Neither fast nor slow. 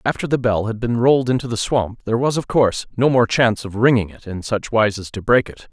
No: fast, 275 wpm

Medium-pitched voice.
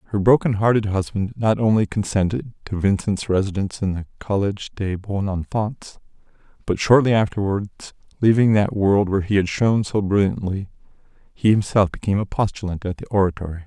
No: low, 100 Hz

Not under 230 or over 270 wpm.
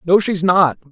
No: average, 200 wpm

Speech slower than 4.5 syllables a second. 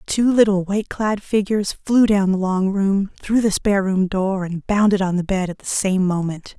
No: 5.1 syllables/s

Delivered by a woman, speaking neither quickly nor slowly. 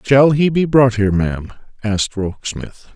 No: male; average, 165 wpm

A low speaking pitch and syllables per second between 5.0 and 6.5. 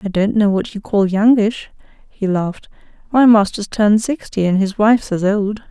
No: high, 205 Hz; 5.1 syllables/s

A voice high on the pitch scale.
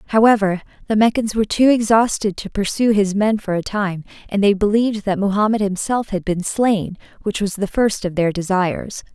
Yes: high, 205 Hz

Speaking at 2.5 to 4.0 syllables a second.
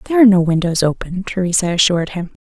No: 7.3 syllables/s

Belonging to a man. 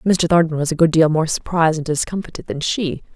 No: female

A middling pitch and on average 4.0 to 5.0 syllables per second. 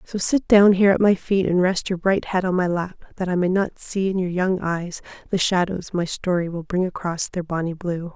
No: medium, 180 Hz; 5.2 syllables/s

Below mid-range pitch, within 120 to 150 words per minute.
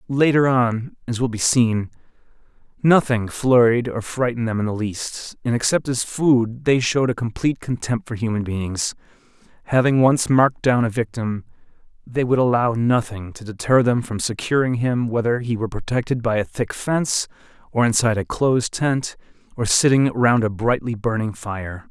No: low, 120 Hz; average, 170 wpm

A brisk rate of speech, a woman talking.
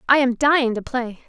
Yes: fast, 235 wpm; female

